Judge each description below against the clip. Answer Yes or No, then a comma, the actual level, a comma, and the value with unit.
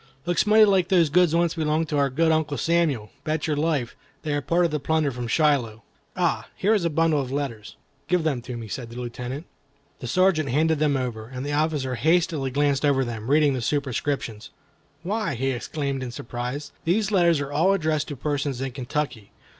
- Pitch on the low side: No, medium, 145 Hz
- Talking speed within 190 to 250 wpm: Yes, fast, 205 wpm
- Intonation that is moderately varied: Yes, average, 4.0 semitones